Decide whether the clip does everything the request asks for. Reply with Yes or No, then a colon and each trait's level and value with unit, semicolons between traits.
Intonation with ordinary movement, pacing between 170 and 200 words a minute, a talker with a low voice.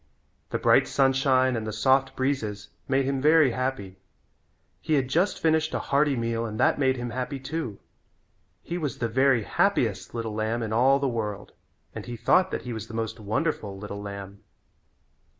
Yes: average, 3.9 semitones; average, 180 wpm; low, 125 Hz